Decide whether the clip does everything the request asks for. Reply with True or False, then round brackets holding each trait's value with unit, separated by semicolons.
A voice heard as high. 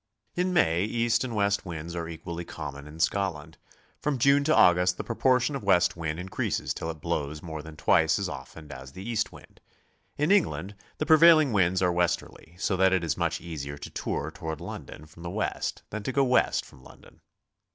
False (90 Hz)